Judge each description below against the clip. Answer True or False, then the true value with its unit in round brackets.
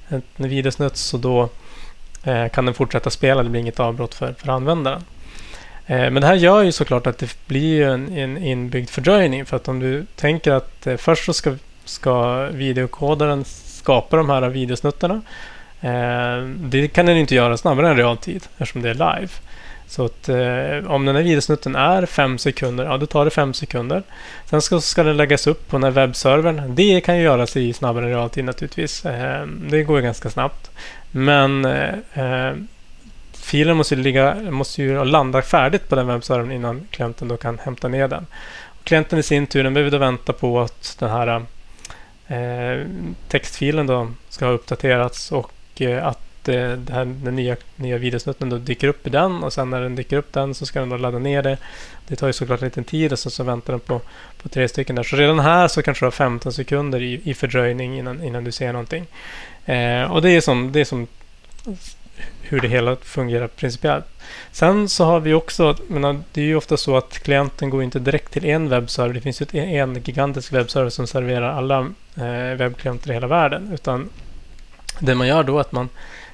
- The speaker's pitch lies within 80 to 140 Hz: True (135 Hz)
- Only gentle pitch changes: False (3.2 semitones)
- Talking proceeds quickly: True (200 wpm)